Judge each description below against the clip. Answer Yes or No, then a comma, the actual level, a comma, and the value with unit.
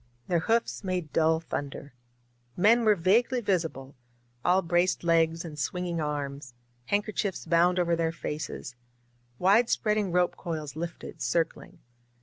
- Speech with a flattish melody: No, average, 3.0 semitones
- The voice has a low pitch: No, medium, 170 Hz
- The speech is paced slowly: Yes, slow, 130 wpm